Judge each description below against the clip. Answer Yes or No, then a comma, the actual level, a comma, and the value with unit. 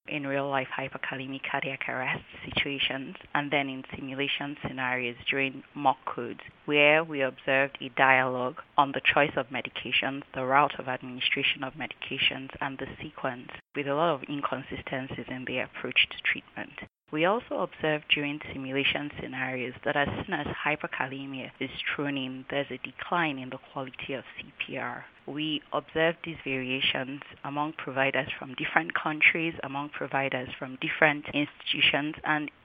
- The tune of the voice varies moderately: No, narrow, 1.9 semitones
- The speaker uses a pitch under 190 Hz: Yes, medium, 140 Hz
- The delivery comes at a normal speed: Yes, average, 150 wpm